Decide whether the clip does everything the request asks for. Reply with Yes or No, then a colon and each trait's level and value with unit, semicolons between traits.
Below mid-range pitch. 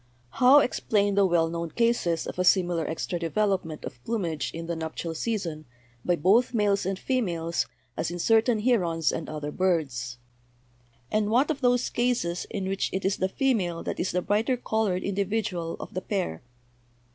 No: medium, 185 Hz